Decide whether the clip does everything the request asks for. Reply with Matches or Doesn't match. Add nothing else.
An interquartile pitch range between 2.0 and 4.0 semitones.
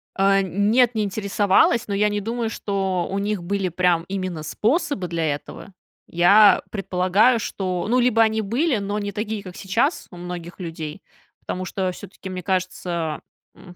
Matches